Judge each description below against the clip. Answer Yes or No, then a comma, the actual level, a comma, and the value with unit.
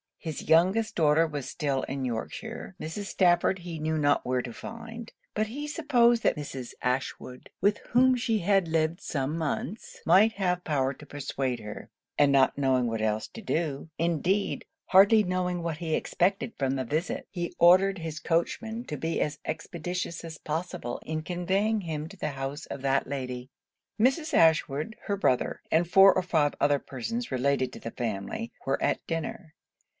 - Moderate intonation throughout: No, wide, 5.7 semitones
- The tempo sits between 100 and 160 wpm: No, average, 170 wpm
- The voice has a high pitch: No, medium, 165 Hz